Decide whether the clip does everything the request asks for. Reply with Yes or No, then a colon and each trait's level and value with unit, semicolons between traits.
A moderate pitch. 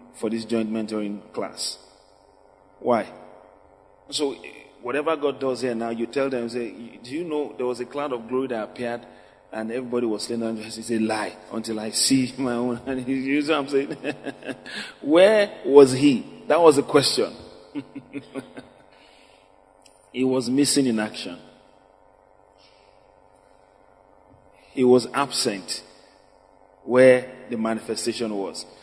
No: low, 125 Hz